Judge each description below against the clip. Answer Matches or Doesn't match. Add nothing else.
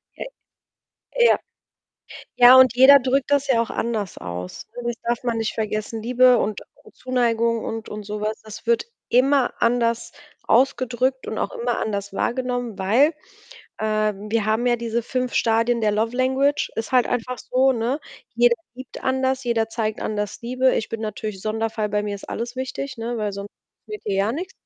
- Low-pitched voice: Doesn't match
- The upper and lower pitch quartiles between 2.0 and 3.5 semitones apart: Matches